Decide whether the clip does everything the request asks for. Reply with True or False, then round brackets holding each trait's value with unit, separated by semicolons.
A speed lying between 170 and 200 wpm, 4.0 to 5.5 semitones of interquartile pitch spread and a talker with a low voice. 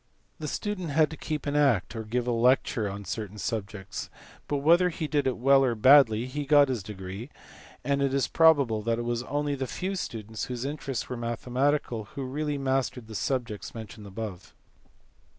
True (185 wpm; 4.3 semitones; 130 Hz)